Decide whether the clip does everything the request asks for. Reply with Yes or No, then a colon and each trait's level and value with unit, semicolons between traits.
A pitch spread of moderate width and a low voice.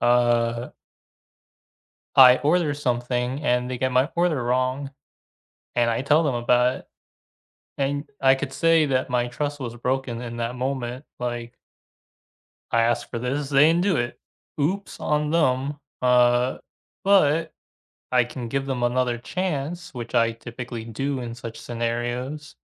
Yes: average, 3.0 semitones; low, 125 Hz